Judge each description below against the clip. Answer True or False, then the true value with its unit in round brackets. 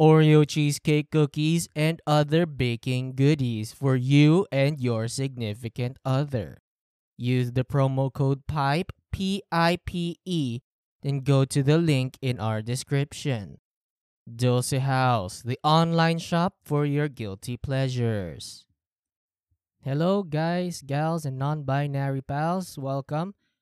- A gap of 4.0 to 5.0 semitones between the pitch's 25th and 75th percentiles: False (3.6 semitones)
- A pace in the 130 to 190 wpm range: False (120 wpm)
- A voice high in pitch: False (140 Hz)